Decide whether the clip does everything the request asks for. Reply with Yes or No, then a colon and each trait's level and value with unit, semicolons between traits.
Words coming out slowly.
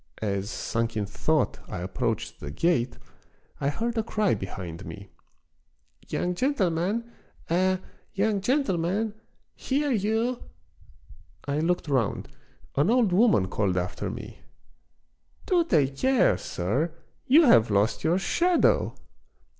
Yes: slow, 130 wpm